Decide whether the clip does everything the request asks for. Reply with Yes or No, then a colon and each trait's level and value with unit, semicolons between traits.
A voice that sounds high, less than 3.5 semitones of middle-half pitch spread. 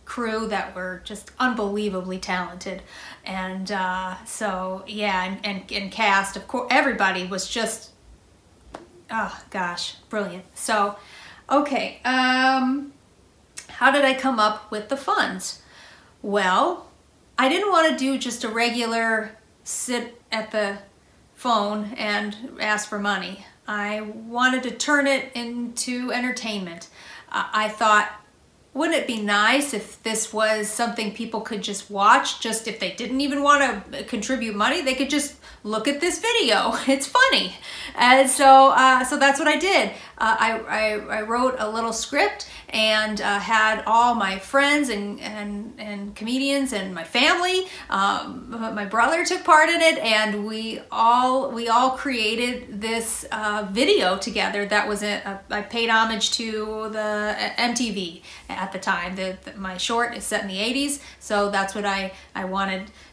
No: high, 220 Hz; average, 3.8 semitones